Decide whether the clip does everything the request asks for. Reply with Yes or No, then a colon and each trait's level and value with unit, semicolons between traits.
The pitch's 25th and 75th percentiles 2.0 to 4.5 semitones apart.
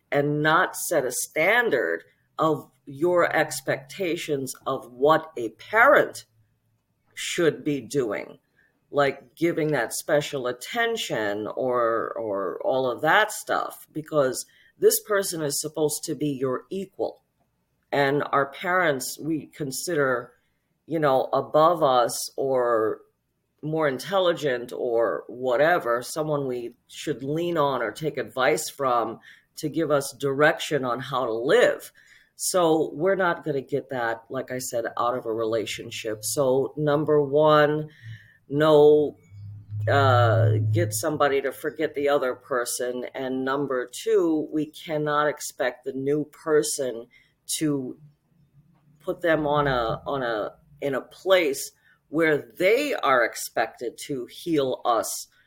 Yes: average, 3.6 semitones